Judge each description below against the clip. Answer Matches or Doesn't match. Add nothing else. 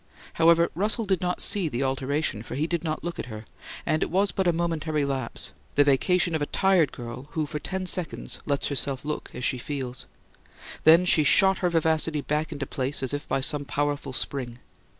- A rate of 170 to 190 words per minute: Doesn't match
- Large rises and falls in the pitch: Doesn't match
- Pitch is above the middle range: Doesn't match